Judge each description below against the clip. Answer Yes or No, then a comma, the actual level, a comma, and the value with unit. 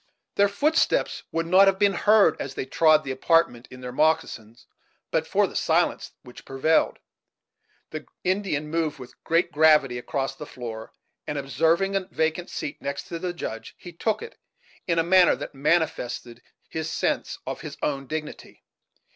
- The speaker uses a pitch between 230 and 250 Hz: No, medium, 155 Hz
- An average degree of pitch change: Yes, average, 4.5 semitones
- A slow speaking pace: No, average, 165 wpm